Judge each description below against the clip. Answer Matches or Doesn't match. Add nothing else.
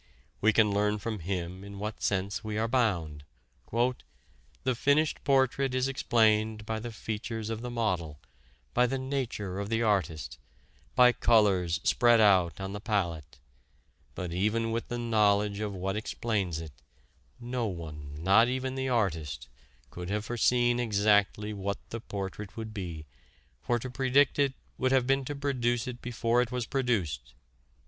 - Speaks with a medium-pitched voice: Doesn't match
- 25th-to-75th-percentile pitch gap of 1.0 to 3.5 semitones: Doesn't match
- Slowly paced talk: Doesn't match